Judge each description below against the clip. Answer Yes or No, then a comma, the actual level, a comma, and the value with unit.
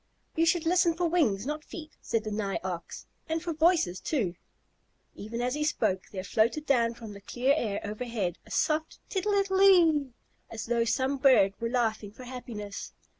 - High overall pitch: Yes, very high, 250 Hz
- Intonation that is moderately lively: No, wide, 6.8 semitones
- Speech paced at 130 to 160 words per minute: No, average, 185 wpm